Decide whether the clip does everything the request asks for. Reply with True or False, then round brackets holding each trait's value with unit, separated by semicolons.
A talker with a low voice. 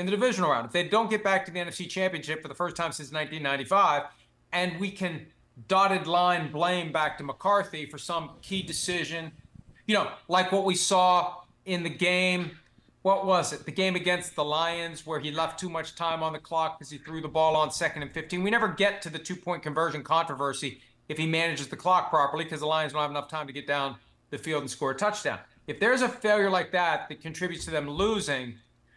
False (165 Hz)